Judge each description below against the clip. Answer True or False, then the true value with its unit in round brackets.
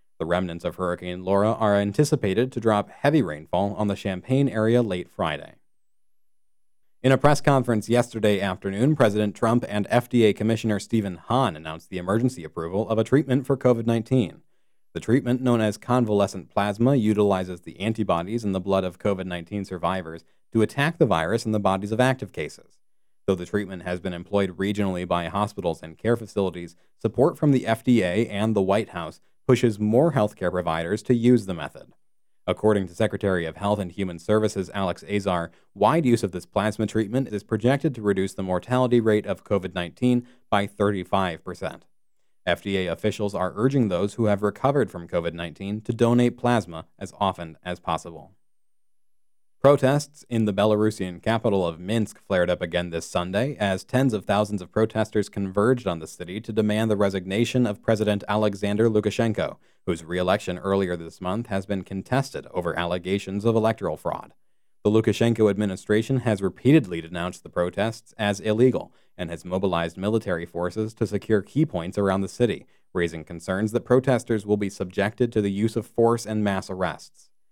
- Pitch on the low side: True (105 Hz)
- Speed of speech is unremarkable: True (170 wpm)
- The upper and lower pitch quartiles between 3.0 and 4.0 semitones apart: True (3.7 semitones)